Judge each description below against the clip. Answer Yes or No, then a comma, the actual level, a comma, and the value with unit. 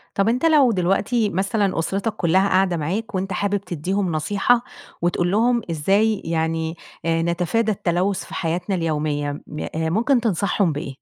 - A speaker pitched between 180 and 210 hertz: Yes, medium, 185 Hz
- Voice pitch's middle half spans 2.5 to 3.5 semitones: No, average, 4.0 semitones